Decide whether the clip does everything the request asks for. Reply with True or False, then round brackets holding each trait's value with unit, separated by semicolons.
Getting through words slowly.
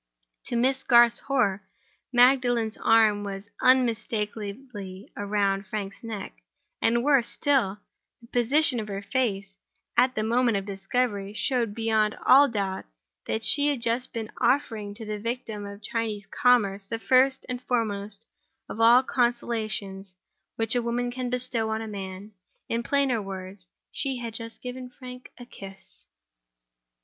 False (145 wpm)